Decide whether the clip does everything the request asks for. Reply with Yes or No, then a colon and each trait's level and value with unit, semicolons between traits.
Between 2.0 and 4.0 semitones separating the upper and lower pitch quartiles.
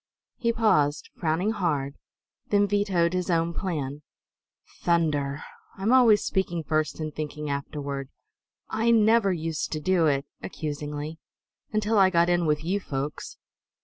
No: average, 4.9 semitones